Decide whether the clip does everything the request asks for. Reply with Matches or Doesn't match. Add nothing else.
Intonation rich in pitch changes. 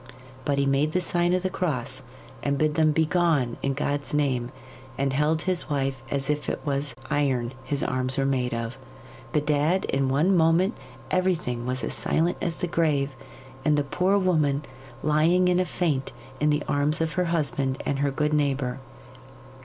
Doesn't match